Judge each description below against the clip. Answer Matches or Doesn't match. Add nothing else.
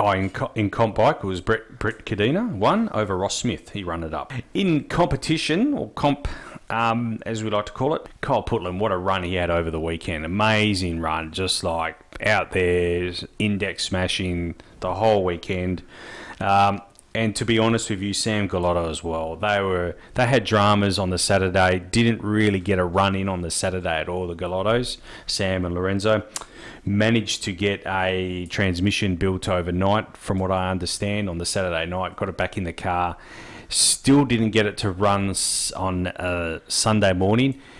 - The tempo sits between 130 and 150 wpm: Doesn't match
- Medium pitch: Doesn't match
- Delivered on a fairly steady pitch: Doesn't match